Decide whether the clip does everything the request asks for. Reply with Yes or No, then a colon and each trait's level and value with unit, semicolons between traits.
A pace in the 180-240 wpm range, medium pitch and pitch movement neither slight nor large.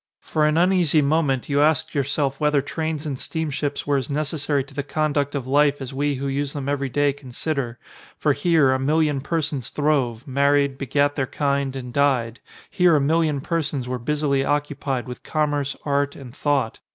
No: average, 185 wpm; medium, 145 Hz; narrow, 1.8 semitones